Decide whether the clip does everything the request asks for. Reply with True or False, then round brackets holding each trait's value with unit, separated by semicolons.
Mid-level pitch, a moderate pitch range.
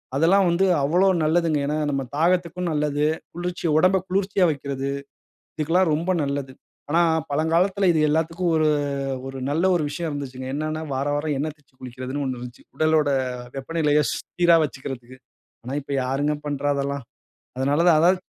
True (150 Hz; 3.4 semitones)